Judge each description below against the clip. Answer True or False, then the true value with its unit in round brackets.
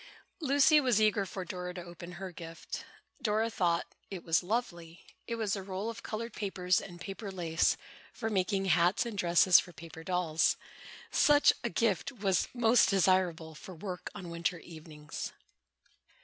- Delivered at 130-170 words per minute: True (160 wpm)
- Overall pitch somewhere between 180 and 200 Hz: True (185 Hz)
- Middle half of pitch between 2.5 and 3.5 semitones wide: False (3.9 semitones)